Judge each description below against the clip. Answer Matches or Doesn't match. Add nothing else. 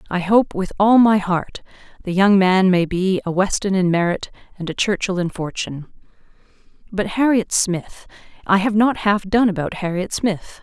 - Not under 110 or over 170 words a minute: Matches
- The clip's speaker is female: Matches